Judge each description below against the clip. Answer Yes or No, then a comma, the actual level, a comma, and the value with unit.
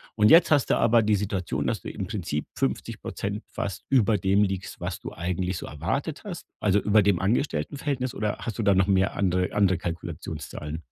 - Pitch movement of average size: Yes, average, 3.3 semitones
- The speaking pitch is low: Yes, low, 100 Hz